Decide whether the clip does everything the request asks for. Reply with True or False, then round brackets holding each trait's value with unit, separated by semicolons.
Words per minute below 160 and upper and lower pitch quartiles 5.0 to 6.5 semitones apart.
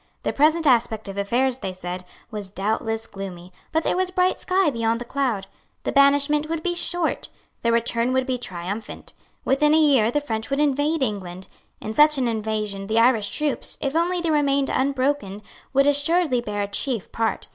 False (185 wpm; 5.5 semitones)